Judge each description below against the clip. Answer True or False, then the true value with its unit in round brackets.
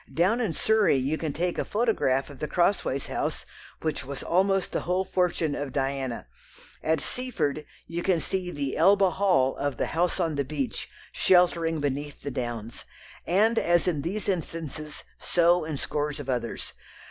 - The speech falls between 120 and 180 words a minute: True (170 wpm)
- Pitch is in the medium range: True (160 Hz)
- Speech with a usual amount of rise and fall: True (4.3 semitones)